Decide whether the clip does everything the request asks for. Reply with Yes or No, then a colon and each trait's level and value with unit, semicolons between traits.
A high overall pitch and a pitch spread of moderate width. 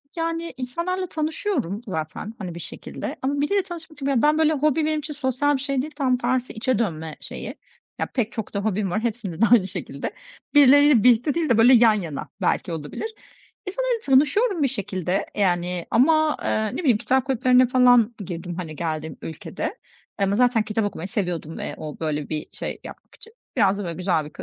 No: high, 240 Hz; wide, 7.7 semitones